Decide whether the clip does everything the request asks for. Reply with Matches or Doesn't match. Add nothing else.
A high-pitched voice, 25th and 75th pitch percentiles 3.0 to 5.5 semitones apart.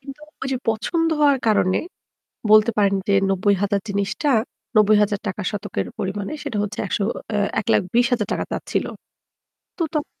Matches